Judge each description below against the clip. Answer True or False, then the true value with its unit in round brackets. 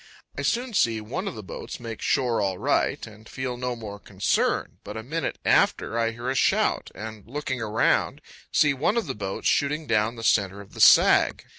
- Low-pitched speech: True (115 Hz)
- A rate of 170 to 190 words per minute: False (200 wpm)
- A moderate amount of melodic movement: True (4.3 semitones)